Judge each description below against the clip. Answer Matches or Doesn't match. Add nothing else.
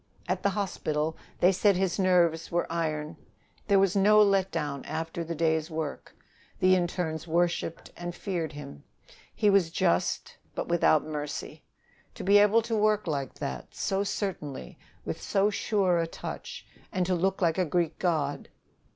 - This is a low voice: Doesn't match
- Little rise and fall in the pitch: Doesn't match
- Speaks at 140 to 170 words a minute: Matches